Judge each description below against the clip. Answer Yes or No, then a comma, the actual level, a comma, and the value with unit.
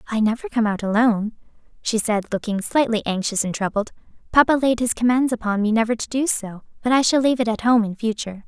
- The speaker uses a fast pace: Yes, fast, 220 wpm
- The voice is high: Yes, high, 225 Hz